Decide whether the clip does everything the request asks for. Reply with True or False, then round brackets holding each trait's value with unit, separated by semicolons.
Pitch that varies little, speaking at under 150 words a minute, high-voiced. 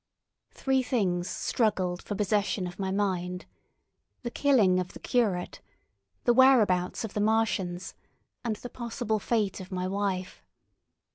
False (3.9 semitones; 135 wpm; 205 Hz)